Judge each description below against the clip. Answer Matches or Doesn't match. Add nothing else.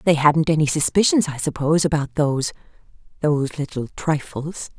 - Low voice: Doesn't match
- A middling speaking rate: Doesn't match